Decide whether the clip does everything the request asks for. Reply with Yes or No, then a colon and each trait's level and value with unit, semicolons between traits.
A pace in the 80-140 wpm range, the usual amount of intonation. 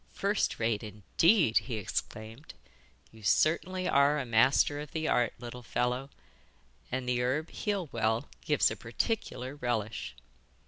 Yes: slow, 135 wpm; average, 5.0 semitones